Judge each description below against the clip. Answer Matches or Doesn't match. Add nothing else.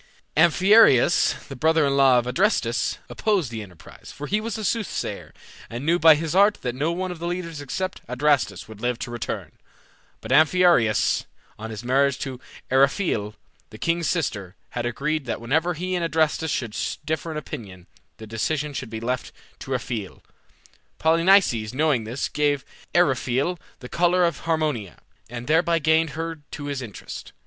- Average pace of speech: Matches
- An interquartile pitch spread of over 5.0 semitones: Matches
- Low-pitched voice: Doesn't match